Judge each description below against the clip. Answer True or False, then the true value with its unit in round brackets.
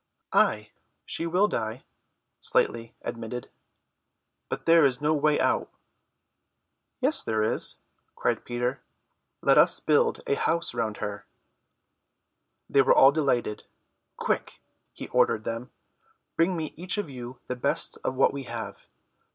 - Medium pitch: False (130 Hz)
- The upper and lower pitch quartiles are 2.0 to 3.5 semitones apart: False (5.5 semitones)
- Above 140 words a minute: False (135 wpm)